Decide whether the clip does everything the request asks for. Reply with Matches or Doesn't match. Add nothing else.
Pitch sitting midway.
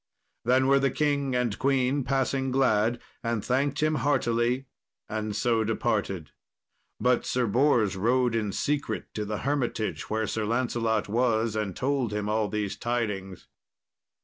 Doesn't match